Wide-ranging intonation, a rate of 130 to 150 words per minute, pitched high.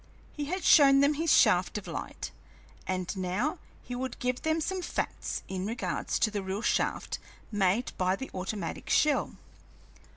No: wide, 7.5 semitones; average, 160 wpm; high, 235 Hz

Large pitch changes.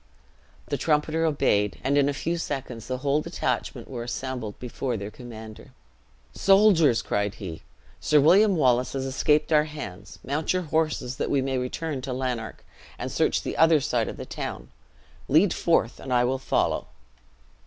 No: average, 4.0 semitones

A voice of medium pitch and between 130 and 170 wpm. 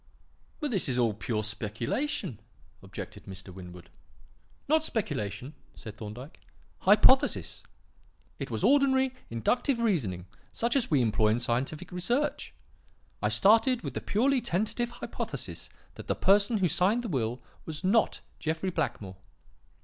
Yes: medium, 170 Hz; slow, 135 wpm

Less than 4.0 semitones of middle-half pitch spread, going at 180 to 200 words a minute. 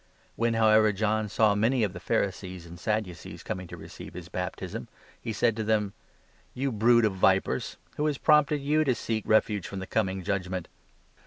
Yes: average, 3.5 semitones; average, 185 wpm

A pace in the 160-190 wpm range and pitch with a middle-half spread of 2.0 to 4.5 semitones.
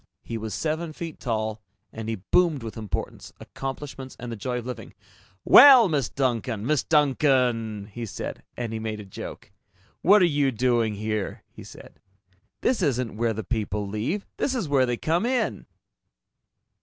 No: average, 170 wpm; average, 5.3 semitones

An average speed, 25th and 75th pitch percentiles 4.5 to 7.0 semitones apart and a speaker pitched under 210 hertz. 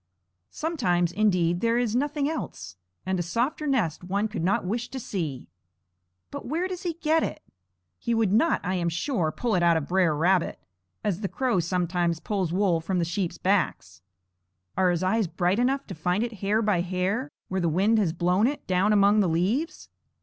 Yes: average, 195 wpm; average, 5.0 semitones; high, 190 Hz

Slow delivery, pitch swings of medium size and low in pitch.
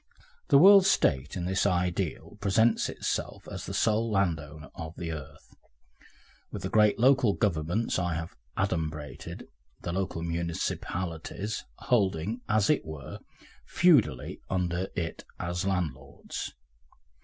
Yes: slow, 120 wpm; average, 4.6 semitones; very low, 90 Hz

